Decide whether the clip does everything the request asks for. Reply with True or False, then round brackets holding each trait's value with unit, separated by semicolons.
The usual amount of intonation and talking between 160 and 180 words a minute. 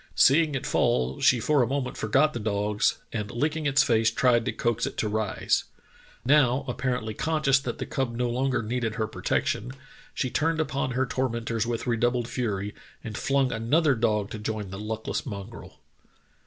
True (3.5 semitones; 175 wpm)